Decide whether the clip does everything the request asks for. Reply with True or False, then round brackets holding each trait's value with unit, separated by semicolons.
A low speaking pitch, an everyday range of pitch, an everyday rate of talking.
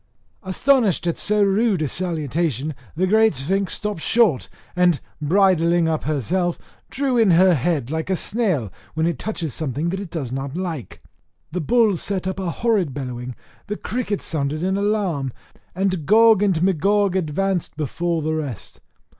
False (175 Hz; 4.4 semitones; 160 wpm)